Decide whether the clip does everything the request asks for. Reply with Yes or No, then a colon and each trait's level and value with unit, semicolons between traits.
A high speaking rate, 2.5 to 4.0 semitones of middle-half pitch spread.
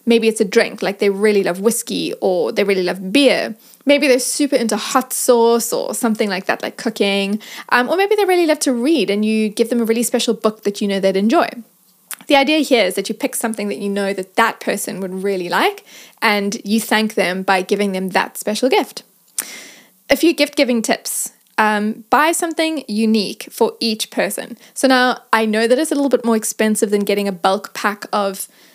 Yes: fast, 215 wpm; average, 3.7 semitones